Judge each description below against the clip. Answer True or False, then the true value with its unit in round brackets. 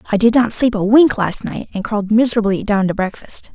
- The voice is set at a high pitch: True (215 Hz)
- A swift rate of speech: True (235 wpm)